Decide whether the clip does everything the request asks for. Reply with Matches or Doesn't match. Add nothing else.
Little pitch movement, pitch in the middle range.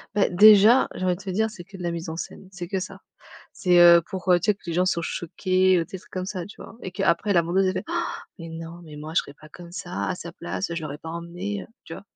Matches